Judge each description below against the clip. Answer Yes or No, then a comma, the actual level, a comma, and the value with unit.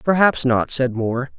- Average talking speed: Yes, average, 175 wpm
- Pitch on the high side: No, low, 135 Hz